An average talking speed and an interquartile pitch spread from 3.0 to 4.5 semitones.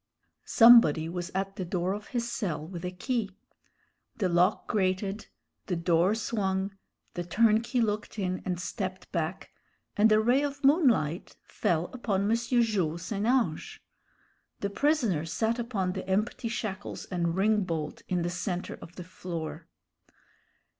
Yes: average, 145 wpm; average, 4.2 semitones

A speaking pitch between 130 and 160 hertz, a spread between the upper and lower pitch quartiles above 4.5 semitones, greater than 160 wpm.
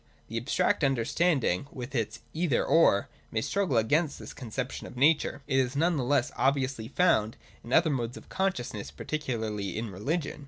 Yes: low, 135 Hz; average, 5.1 semitones; average, 185 wpm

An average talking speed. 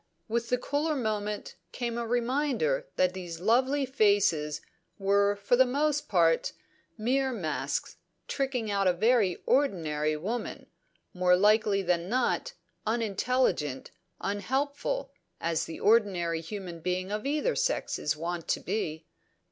No: slow, 130 wpm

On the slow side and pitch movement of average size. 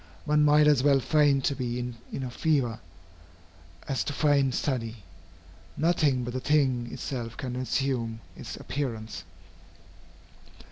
Yes: slow, 130 wpm; average, 3.2 semitones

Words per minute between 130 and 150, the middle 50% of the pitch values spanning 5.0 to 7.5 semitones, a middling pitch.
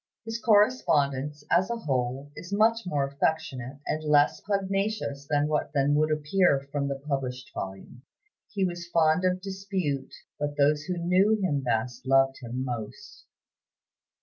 Yes: average, 140 wpm; average, 5.3 semitones; medium, 150 Hz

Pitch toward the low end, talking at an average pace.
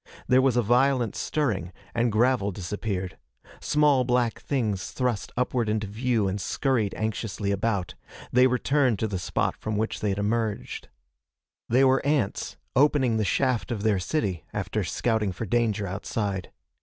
Yes: low, 110 Hz; average, 155 wpm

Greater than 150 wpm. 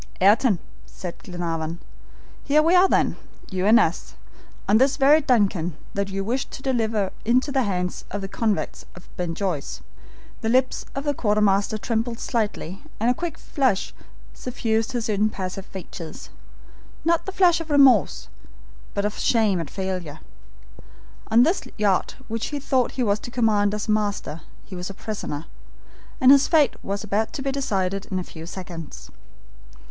Yes: average, 165 wpm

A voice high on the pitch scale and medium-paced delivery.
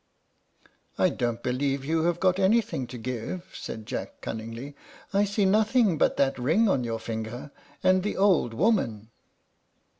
No: medium, 140 Hz; average, 150 wpm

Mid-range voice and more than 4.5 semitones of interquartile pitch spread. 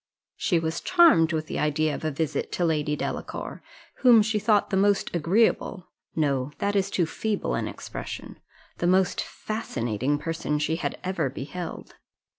Yes: medium, 165 Hz; average, 4.9 semitones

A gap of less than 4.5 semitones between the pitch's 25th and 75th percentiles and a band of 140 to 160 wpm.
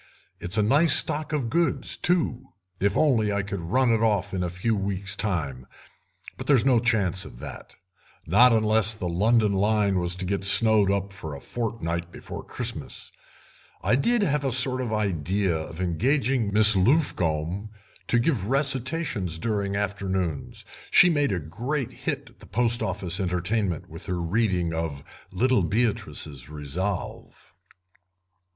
No: average, 5.0 semitones; average, 150 wpm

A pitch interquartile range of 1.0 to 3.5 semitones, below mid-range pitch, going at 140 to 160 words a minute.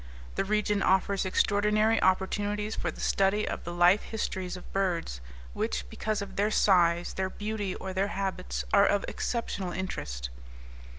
No: average, 2.7 semitones; high, 195 Hz; average, 155 wpm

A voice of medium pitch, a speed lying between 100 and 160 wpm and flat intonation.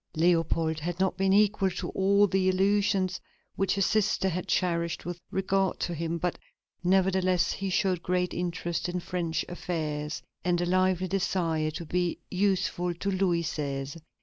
Yes: medium, 180 Hz; average, 155 wpm; narrow, 2.1 semitones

